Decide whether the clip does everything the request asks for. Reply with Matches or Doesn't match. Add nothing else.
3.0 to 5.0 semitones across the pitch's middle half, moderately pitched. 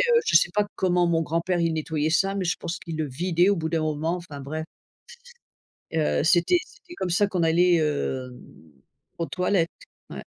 Doesn't match